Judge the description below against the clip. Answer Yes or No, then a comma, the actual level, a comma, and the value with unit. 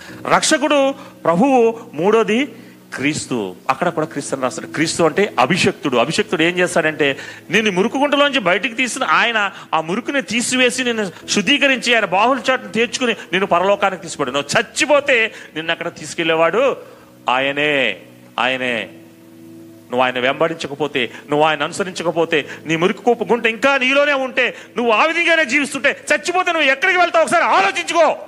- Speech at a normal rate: No, fast, 130 wpm